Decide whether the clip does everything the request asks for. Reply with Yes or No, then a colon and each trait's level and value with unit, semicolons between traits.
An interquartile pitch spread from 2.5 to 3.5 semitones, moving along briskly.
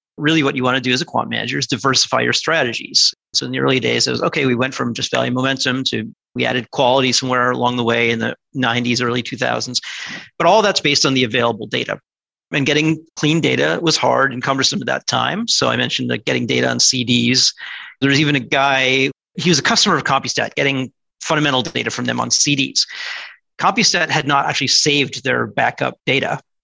Yes: average, 2.9 semitones; fast, 215 wpm